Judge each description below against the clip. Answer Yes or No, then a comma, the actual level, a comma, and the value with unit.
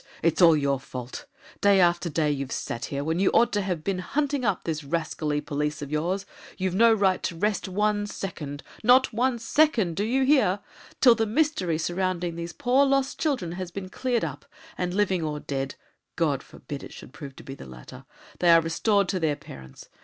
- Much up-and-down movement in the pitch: Yes, wide, 5.7 semitones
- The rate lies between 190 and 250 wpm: Yes, average, 200 wpm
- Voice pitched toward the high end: No, medium, 180 Hz